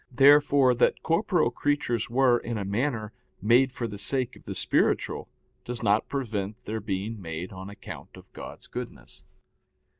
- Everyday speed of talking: Yes, average, 155 wpm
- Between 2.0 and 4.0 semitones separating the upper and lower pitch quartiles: No, average, 4.5 semitones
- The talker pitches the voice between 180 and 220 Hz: No, low, 115 Hz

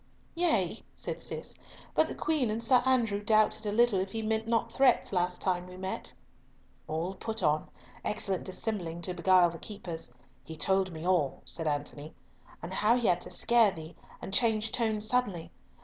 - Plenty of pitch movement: No, average, 4.2 semitones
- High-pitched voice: Yes, high, 195 Hz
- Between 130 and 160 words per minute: No, average, 175 wpm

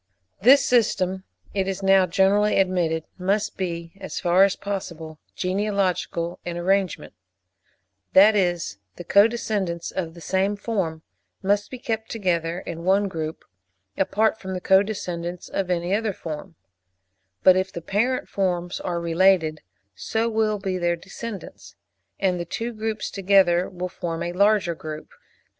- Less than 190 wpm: Yes, average, 145 wpm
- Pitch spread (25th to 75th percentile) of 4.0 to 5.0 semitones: No, average, 2.9 semitones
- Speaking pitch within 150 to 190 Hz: Yes, medium, 185 Hz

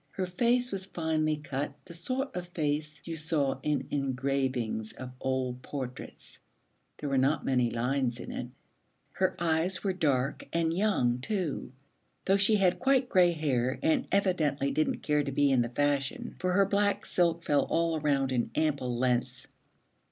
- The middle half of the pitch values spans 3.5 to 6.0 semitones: Yes, average, 5.2 semitones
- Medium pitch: Yes, medium, 150 Hz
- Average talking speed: Yes, average, 165 wpm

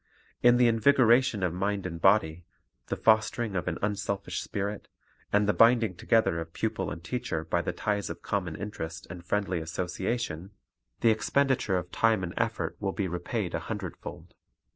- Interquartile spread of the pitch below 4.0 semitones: No, average, 4.3 semitones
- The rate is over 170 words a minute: No, average, 165 wpm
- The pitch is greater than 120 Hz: No, low, 100 Hz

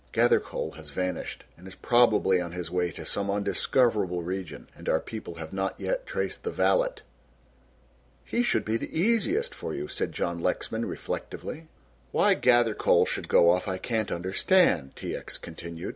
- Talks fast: No, average, 165 wpm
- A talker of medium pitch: No, low, 100 Hz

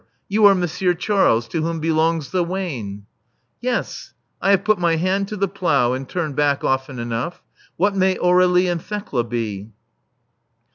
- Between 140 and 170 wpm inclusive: Yes, average, 160 wpm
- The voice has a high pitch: No, medium, 170 Hz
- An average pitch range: No, wide, 6.2 semitones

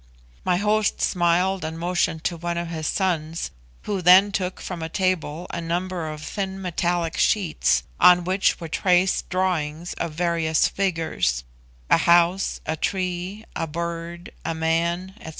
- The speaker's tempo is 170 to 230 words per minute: No, average, 150 wpm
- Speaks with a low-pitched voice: No, medium, 175 Hz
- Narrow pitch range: Yes, narrow, 2.1 semitones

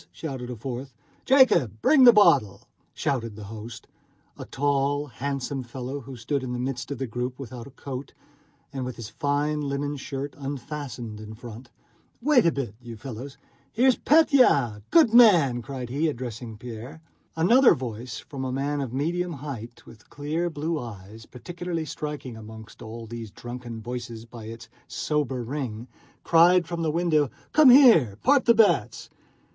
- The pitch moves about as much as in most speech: Yes, average, 4.6 semitones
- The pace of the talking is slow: No, average, 160 wpm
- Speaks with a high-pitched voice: No, low, 135 Hz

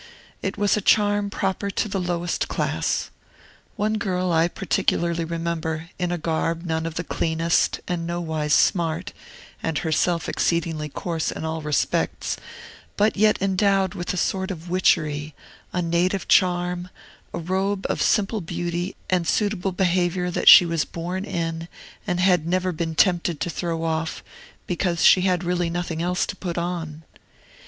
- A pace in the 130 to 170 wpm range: Yes, average, 155 wpm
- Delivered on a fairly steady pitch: Yes, narrow, 2.1 semitones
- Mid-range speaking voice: Yes, medium, 175 Hz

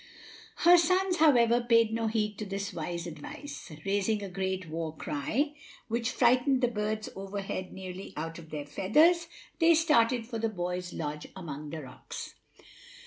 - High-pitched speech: Yes, high, 210 Hz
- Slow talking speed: No, average, 155 wpm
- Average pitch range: No, wide, 5.7 semitones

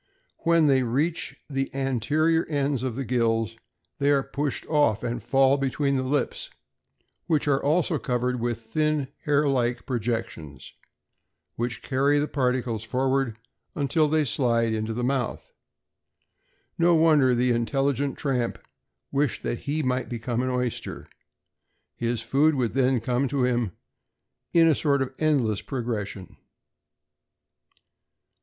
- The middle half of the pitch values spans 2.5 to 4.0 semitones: Yes, average, 3.2 semitones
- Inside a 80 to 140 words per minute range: Yes, slow, 135 wpm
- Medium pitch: No, low, 130 Hz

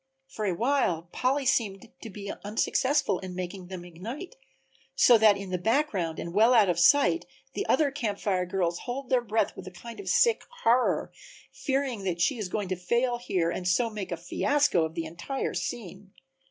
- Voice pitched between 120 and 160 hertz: No, high, 210 Hz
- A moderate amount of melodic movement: No, wide, 5.8 semitones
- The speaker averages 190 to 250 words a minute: Yes, average, 195 wpm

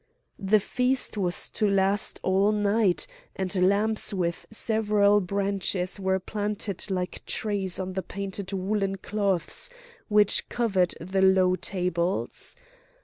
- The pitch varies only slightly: Yes, narrow, 1.8 semitones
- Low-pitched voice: No, high, 195 Hz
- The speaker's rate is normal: No, slow, 120 wpm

